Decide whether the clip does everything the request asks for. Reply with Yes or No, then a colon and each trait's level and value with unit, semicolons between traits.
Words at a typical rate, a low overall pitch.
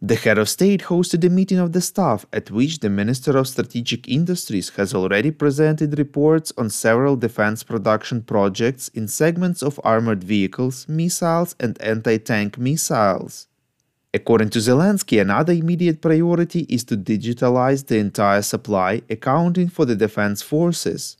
Yes: average, 150 wpm; low, 130 Hz